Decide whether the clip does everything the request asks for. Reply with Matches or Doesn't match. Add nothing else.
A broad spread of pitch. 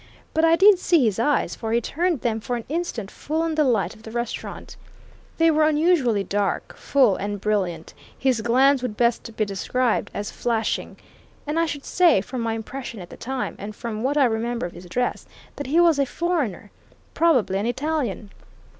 Matches